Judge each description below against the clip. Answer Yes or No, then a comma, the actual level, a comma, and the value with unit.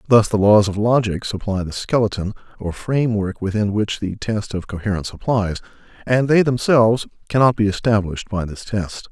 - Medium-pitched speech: No, low, 105 Hz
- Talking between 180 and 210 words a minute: No, average, 170 wpm